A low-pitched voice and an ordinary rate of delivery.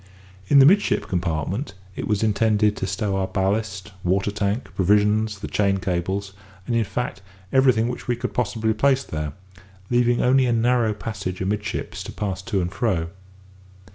Yes: low, 105 Hz; average, 165 wpm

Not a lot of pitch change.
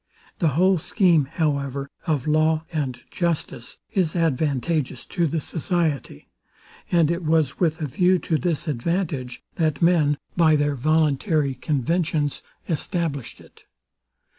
No: average, 3.1 semitones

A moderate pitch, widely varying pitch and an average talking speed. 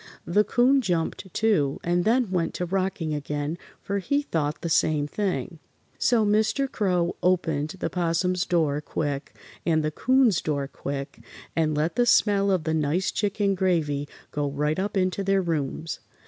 No: medium, 175 Hz; average, 4.6 semitones; average, 160 wpm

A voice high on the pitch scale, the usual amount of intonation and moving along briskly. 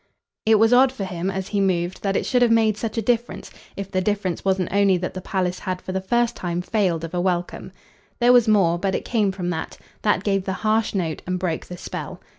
Yes: high, 195 Hz; average, 3.2 semitones; fast, 240 wpm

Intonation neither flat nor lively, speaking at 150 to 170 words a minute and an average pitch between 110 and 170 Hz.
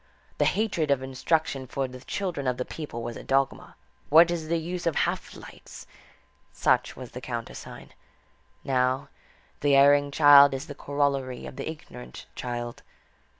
Yes: average, 3.4 semitones; average, 155 wpm; medium, 140 Hz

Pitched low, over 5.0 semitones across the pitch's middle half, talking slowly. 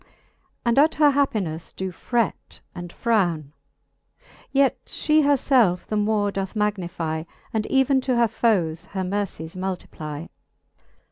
No: high, 205 Hz; wide, 5.6 semitones; slow, 130 wpm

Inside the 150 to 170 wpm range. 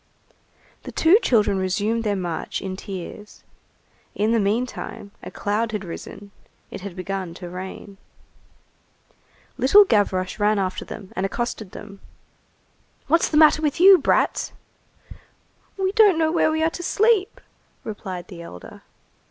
No: average, 140 wpm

